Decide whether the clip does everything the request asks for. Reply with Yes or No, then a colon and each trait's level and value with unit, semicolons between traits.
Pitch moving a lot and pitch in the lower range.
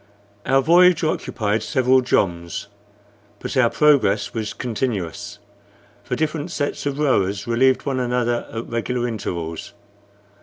No: average, 4.3 semitones; low, 120 Hz